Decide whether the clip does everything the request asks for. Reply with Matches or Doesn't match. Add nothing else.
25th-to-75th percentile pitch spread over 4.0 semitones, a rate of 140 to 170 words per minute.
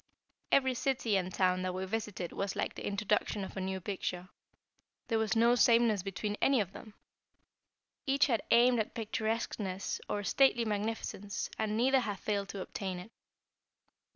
Doesn't match